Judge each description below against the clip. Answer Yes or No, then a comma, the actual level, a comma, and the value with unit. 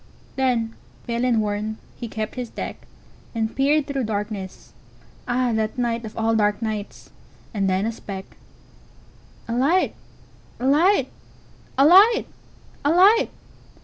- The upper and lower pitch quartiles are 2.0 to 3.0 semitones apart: No, average, 4.1 semitones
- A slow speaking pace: Yes, slow, 120 wpm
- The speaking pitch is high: Yes, high, 230 Hz